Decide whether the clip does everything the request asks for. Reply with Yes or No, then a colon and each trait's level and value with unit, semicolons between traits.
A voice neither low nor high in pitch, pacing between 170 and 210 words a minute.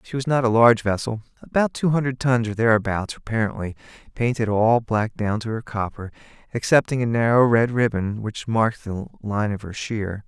No: low, 115 Hz; average, 185 wpm